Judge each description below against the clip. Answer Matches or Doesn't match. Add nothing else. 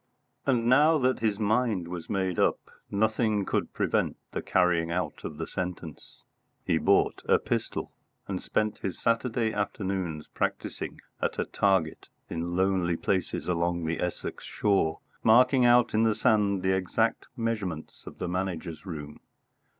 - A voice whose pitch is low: Matches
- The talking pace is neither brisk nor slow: Matches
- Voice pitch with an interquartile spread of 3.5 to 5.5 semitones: Matches